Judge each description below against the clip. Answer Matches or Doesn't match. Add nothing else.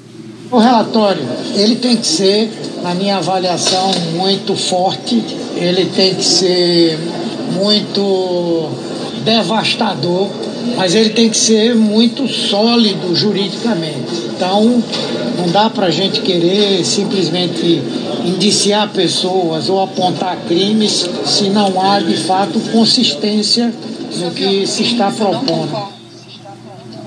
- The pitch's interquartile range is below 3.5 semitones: Matches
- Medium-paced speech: Doesn't match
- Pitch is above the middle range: Matches